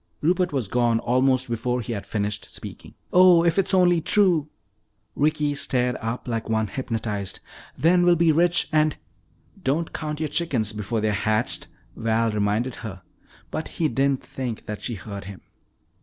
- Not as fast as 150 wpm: No, average, 165 wpm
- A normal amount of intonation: No, wide, 6.2 semitones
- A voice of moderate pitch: No, low, 125 Hz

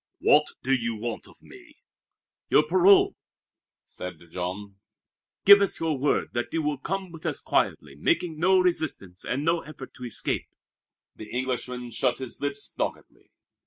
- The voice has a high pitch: No, low, 135 Hz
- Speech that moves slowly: No, average, 155 wpm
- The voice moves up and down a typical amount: No, wide, 5.8 semitones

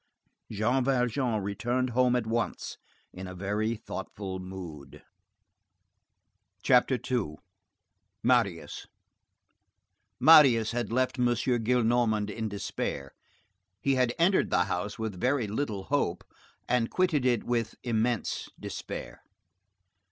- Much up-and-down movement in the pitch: No, average, 3.8 semitones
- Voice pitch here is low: Yes, low, 115 Hz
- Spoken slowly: Yes, slow, 105 wpm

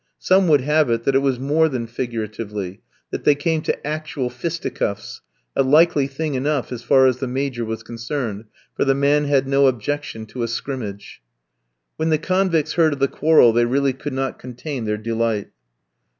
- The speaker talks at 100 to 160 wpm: No, average, 185 wpm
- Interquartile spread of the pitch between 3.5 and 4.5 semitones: Yes, average, 4.0 semitones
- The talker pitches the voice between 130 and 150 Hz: Yes, low, 135 Hz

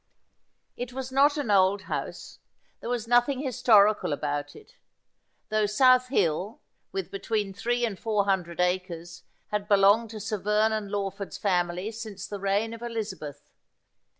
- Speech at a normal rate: Yes, average, 145 wpm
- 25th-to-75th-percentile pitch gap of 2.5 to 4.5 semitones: Yes, average, 3.3 semitones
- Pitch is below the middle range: No, high, 210 Hz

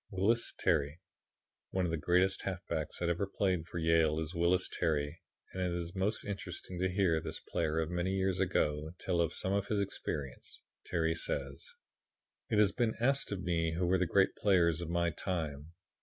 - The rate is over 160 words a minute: Yes, average, 185 wpm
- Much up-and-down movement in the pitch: No, average, 2.7 semitones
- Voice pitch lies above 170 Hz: No, very low, 90 Hz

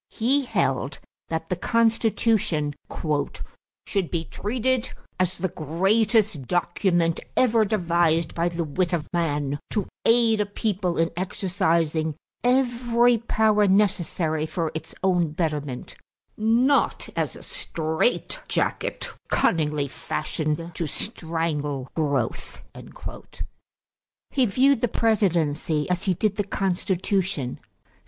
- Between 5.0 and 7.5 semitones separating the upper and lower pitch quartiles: Yes, average, 5.3 semitones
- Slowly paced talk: Yes, slow, 110 wpm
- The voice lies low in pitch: No, medium, 180 Hz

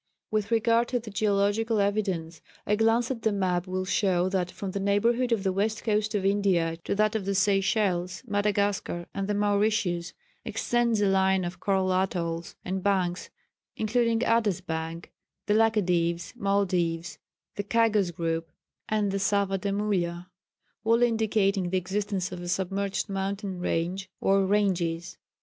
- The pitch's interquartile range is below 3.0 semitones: Yes, narrow, 2.6 semitones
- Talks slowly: No, average, 155 wpm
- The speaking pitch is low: No, high, 195 Hz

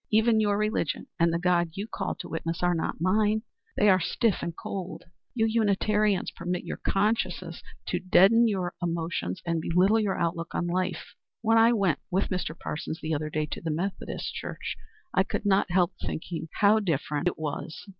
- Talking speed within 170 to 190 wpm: Yes, average, 185 wpm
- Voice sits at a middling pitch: Yes, medium, 180 Hz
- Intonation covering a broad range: No, average, 3.7 semitones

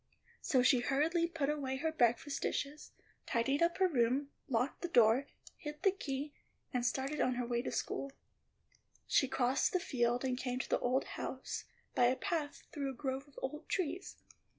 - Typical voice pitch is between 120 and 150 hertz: No, very high, 270 Hz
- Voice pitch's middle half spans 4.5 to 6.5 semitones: No, average, 3.2 semitones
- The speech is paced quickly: No, average, 180 wpm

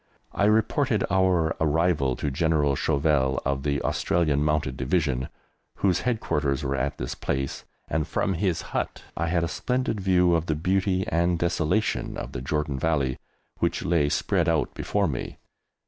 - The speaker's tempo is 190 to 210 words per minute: No, average, 160 wpm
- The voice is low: Yes, very low, 80 Hz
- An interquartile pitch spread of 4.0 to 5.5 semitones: Yes, average, 4.4 semitones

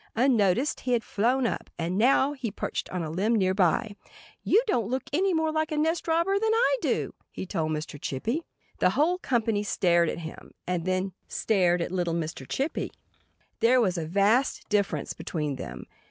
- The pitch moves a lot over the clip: Yes, wide, 7.6 semitones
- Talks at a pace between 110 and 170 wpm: No, average, 185 wpm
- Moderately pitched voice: No, high, 215 Hz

